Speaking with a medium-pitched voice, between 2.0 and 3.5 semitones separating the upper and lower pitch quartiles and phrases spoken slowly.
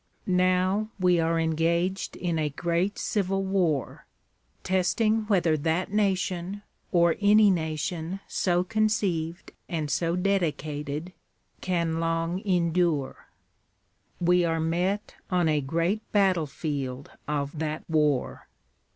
Yes: medium, 170 Hz; average, 2.9 semitones; slow, 110 wpm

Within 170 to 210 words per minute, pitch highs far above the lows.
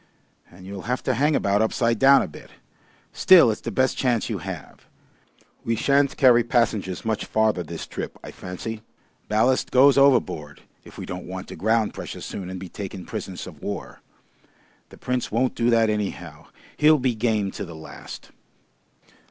No: average, 175 wpm; average, 4.6 semitones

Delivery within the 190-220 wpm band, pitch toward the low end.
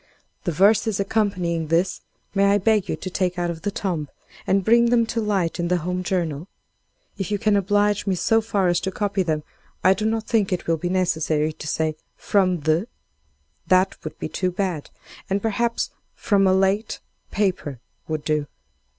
No: average, 195 wpm; medium, 185 Hz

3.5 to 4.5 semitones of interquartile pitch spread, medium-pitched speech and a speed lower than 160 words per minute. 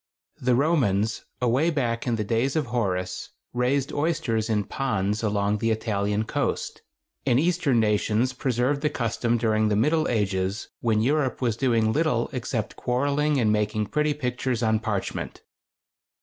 No: average, 4.0 semitones; low, 120 Hz; average, 150 wpm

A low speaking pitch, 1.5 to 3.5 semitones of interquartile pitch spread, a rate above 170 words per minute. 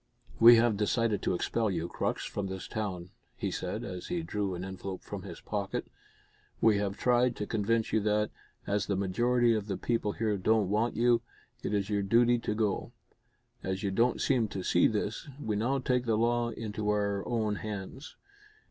Yes: low, 105 Hz; average, 2.9 semitones; average, 190 wpm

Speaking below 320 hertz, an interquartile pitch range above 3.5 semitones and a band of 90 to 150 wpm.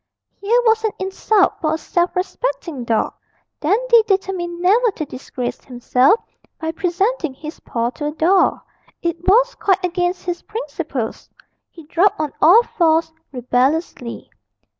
No: very high, 345 Hz; average, 4.7 semitones; average, 140 wpm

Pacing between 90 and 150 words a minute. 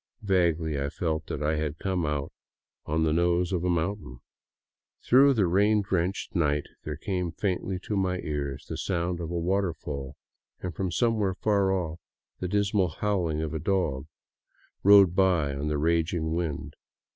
No: average, 165 wpm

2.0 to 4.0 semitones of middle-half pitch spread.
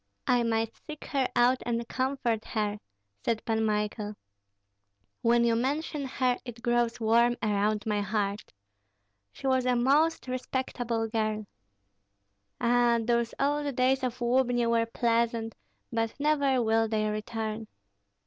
Yes: narrow, 2.4 semitones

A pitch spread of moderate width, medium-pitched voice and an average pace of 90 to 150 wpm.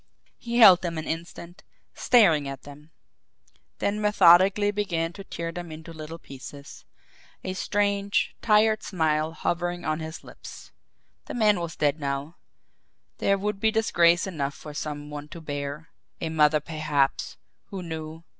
Yes: average, 4.4 semitones; medium, 165 Hz; average, 145 wpm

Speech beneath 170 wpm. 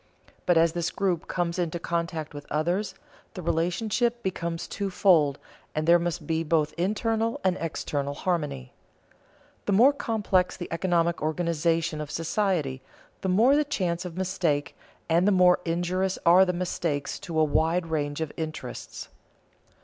Yes: average, 150 wpm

